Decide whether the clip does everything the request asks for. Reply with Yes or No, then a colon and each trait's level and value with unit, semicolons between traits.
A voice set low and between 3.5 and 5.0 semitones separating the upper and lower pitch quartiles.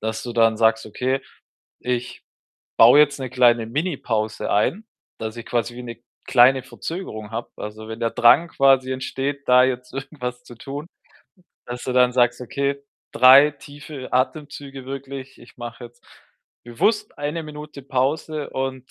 No: low, 130 Hz; average, 2.8 semitones